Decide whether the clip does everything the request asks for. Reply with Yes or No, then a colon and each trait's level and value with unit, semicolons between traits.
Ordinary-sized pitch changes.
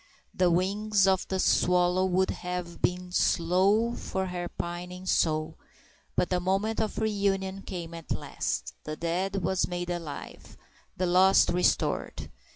No: narrow, 1.6 semitones